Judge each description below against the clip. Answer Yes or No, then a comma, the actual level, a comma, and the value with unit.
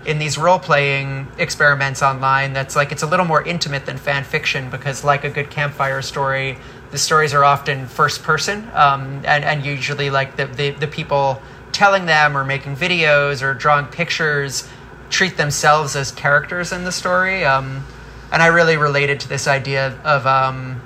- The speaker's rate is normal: Yes, average, 180 wpm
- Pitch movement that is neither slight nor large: No, narrow, 2.1 semitones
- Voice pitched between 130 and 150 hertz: Yes, medium, 140 Hz